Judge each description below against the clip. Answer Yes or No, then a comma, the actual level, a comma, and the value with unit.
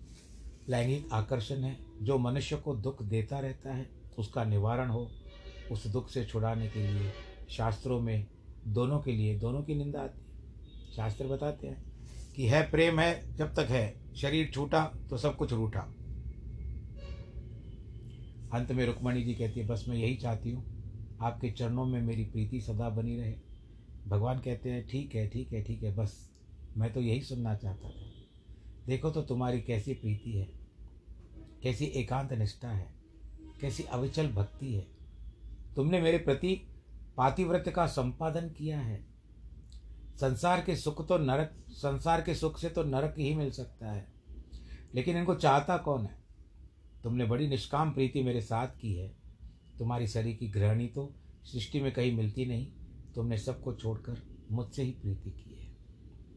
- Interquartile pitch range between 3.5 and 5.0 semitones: Yes, average, 4.3 semitones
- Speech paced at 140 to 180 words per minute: Yes, average, 160 wpm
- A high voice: No, low, 120 Hz